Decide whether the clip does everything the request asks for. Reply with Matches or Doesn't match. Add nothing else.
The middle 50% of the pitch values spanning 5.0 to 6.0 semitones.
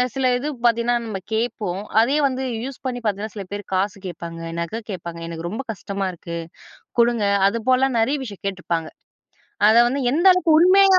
Matches